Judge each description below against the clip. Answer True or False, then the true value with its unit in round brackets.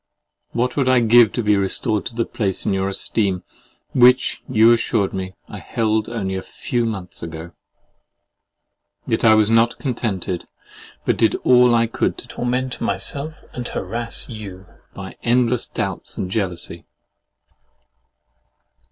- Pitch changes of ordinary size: True (3.8 semitones)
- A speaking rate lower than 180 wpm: True (145 wpm)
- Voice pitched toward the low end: True (115 Hz)